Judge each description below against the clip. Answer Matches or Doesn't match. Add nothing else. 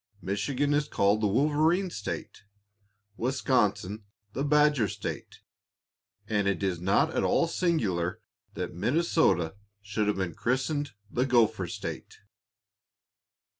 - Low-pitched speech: Matches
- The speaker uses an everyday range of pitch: Doesn't match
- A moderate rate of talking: Doesn't match